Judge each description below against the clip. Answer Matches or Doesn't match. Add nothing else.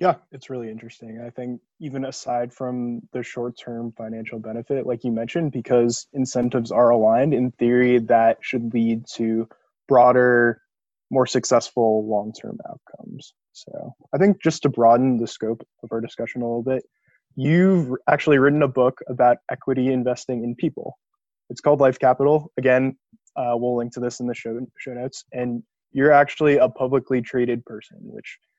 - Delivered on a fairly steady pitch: Matches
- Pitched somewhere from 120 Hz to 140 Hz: Matches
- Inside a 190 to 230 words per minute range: Doesn't match